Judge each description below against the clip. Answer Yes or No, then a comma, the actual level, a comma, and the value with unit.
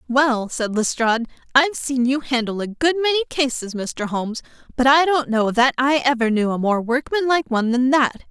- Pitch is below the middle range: No, very high, 255 Hz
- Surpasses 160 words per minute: Yes, average, 195 wpm